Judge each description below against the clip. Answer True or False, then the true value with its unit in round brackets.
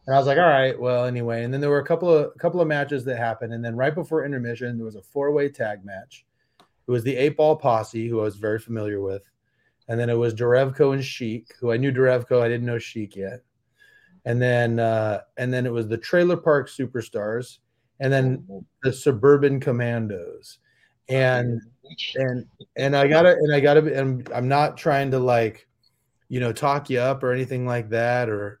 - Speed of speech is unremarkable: False (210 wpm)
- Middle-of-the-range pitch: False (125 Hz)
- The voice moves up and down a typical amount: True (3.0 semitones)